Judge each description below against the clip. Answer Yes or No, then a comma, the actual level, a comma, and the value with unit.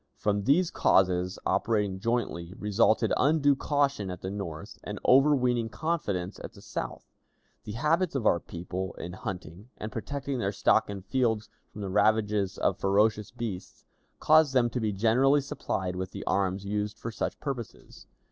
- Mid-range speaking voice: No, low, 105 Hz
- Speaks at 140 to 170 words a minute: Yes, average, 160 wpm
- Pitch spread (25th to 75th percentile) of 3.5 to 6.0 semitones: Yes, average, 4.9 semitones